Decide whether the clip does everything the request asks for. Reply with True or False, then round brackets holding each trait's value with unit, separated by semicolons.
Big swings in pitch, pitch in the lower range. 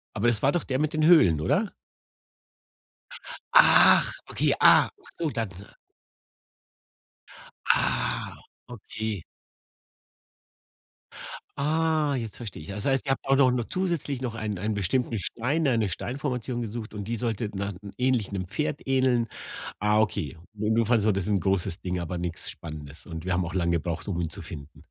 True (6.1 semitones; 110 Hz)